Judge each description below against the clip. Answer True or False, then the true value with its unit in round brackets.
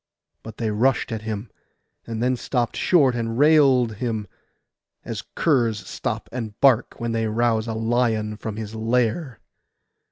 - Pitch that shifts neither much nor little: False (2.2 semitones)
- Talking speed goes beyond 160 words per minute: False (150 wpm)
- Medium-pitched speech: False (115 Hz)